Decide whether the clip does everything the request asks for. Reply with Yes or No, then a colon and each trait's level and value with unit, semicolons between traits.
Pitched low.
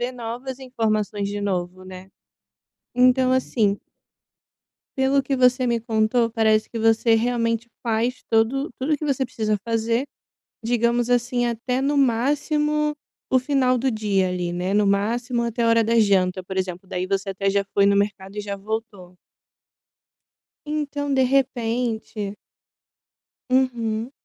No: high, 230 Hz